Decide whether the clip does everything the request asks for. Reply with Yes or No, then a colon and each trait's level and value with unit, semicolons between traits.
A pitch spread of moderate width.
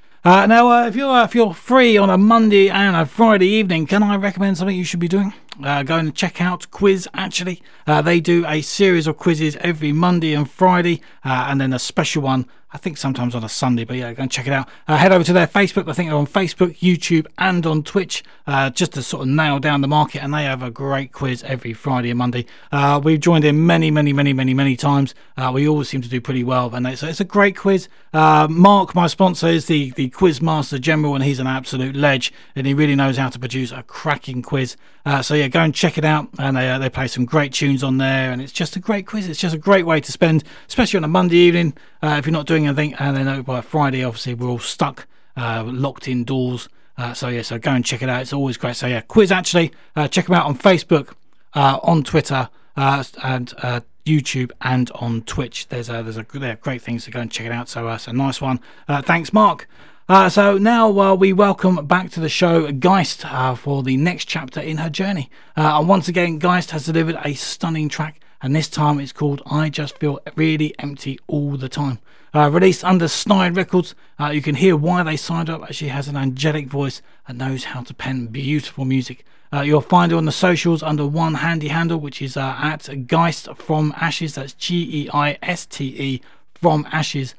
Yes: average, 4.5 semitones